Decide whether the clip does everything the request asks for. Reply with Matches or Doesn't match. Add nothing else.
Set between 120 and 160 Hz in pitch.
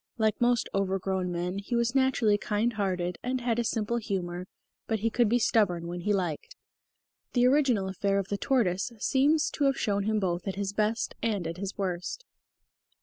Doesn't match